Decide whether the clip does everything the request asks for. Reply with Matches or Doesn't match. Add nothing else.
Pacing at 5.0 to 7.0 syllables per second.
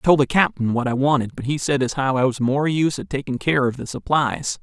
Matches